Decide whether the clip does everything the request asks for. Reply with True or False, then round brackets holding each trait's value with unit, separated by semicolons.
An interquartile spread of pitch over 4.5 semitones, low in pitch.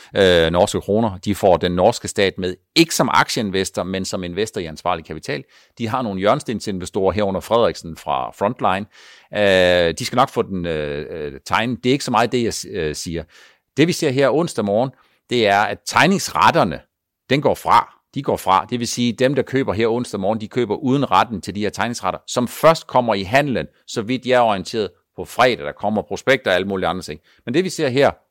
True (5.4 semitones; 110 Hz)